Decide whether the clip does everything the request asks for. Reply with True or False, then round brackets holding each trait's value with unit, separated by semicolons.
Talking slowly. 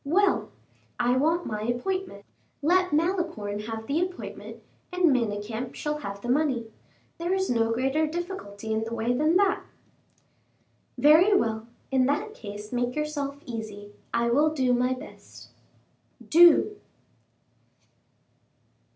True (125 wpm)